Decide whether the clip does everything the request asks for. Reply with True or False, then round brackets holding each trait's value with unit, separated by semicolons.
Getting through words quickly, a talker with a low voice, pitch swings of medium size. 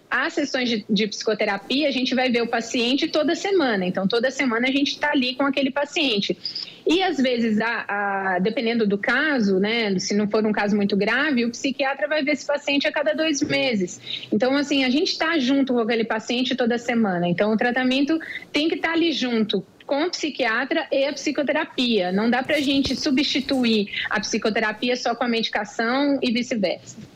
False (195 wpm; 255 Hz; 4.5 semitones)